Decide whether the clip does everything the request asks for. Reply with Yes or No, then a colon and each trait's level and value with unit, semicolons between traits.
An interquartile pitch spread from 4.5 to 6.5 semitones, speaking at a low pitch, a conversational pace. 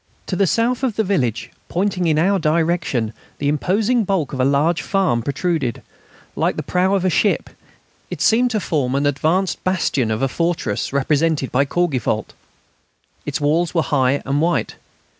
No: average, 5.2 semitones; medium, 160 Hz; average, 170 wpm